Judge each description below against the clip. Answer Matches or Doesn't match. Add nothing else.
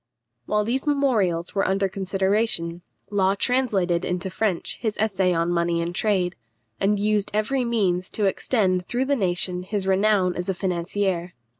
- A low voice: Doesn't match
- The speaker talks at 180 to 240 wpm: Doesn't match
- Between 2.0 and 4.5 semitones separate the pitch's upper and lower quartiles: Matches